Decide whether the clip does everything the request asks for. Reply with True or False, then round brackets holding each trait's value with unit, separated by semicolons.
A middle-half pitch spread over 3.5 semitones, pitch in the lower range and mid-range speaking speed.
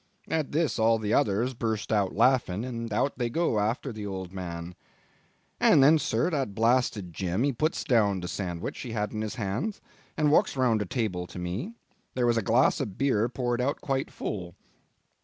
True (4.5 semitones; 115 Hz; 195 wpm)